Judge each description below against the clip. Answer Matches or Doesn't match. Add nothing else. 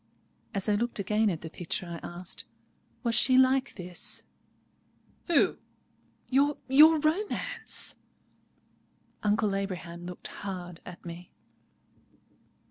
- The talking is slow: Matches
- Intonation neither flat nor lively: Doesn't match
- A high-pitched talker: Matches